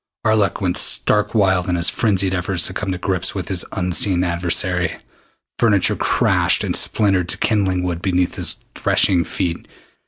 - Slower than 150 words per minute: No, average, 160 wpm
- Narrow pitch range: Yes, narrow, 1.8 semitones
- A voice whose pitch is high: No, very low, 90 Hz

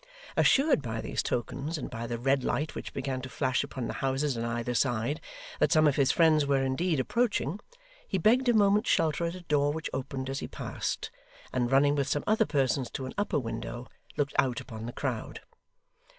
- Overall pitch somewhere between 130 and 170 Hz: Yes, medium, 140 Hz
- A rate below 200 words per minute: No, fast, 205 wpm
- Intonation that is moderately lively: Yes, average, 3.8 semitones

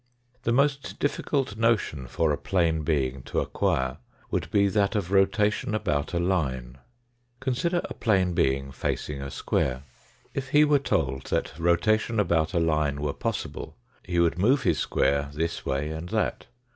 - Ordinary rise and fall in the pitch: No, wide, 7.1 semitones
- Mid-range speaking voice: No, very low, 85 Hz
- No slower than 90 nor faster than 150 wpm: No, average, 160 wpm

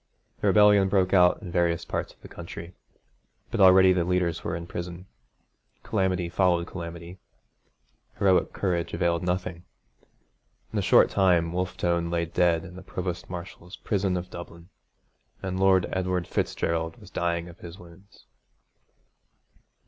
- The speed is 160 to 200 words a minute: No, average, 145 wpm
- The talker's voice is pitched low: Yes, very low, 90 Hz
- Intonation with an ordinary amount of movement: No, narrow, 1.6 semitones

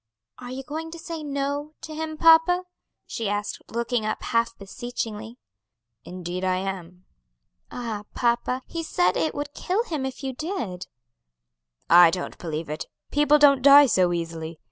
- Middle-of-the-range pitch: No, high, 240 Hz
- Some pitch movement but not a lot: No, wide, 8.1 semitones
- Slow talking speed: No, average, 155 wpm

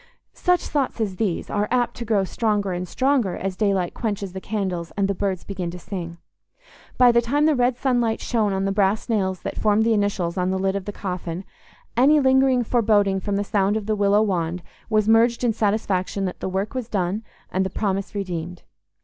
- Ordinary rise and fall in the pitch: Yes, average, 3.3 semitones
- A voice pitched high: Yes, high, 205 Hz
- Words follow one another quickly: Yes, fast, 210 wpm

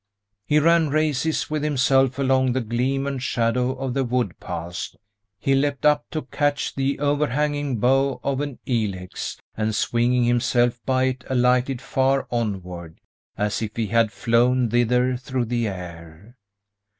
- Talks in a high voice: No, low, 125 Hz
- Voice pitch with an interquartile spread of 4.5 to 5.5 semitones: No, average, 2.9 semitones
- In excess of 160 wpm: No, average, 150 wpm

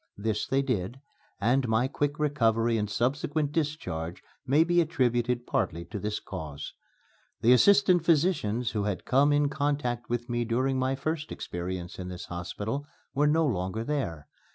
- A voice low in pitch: Yes, low, 125 Hz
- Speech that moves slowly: No, average, 155 wpm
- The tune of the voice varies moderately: No, wide, 5.7 semitones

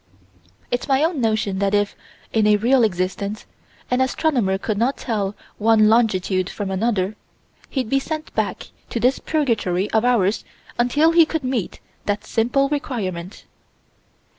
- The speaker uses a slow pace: No, average, 145 wpm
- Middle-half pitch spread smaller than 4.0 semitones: No, average, 4.6 semitones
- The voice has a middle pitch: No, high, 225 Hz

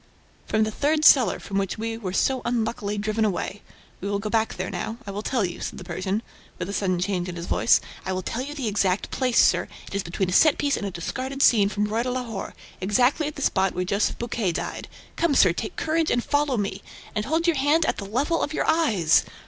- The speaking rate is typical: No, fast, 245 wpm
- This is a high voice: Yes, high, 215 Hz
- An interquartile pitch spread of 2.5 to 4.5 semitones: No, wide, 5.4 semitones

